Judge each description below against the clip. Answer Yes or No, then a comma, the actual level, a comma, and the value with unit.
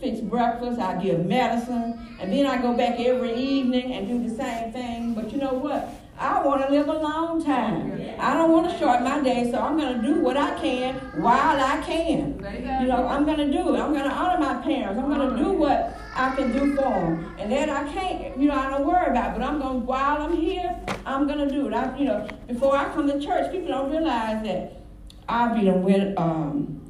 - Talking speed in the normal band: No, fast, 240 wpm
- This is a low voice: No, very high, 265 Hz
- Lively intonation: No, average, 3.5 semitones